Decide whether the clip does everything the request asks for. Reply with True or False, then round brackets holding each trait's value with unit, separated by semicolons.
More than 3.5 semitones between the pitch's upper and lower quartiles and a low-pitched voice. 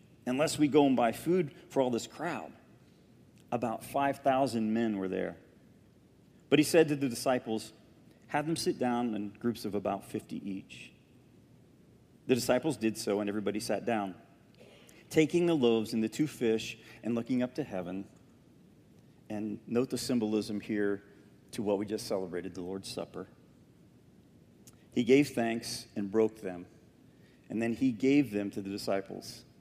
True (4.4 semitones; 115 Hz)